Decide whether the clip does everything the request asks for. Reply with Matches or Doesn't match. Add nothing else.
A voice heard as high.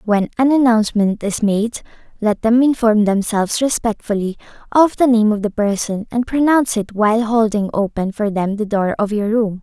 Matches